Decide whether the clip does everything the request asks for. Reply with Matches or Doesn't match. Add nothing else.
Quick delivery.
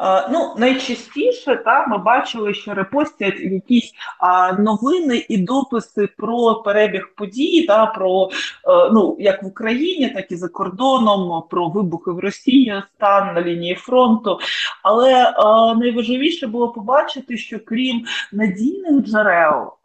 Doesn't match